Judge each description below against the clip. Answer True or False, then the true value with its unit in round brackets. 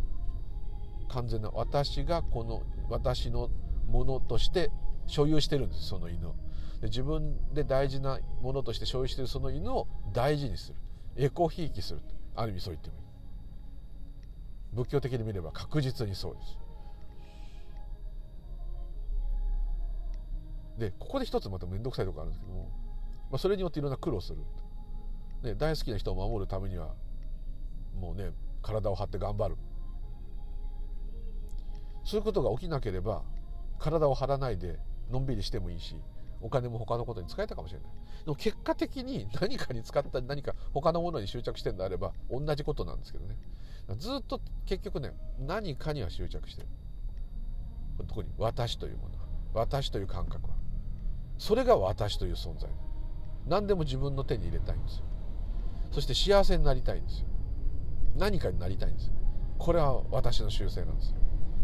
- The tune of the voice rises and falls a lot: True (7.0 semitones)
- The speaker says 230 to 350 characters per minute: True (325 characters per minute)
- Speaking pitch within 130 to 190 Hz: False (105 Hz)